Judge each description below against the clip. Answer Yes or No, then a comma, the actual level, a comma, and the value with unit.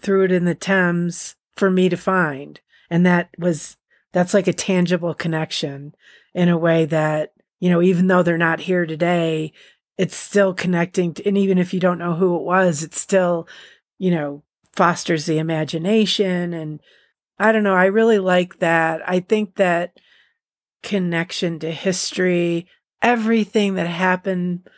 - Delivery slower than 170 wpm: Yes, average, 160 wpm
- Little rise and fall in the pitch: Yes, narrow, 2.3 semitones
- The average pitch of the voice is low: No, medium, 180 Hz